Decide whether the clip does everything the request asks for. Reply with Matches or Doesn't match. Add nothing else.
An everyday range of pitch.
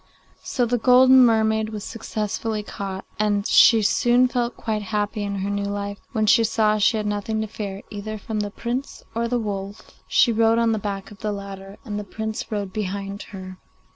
Doesn't match